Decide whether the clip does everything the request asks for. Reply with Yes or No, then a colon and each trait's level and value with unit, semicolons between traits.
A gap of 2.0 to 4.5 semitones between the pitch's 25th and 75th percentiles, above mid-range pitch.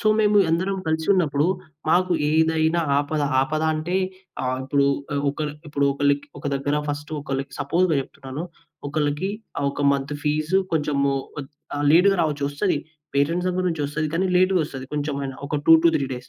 No: average, 2.8 semitones; medium, 150 Hz